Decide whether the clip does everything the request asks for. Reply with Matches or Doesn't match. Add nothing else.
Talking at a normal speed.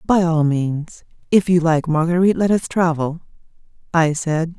Matches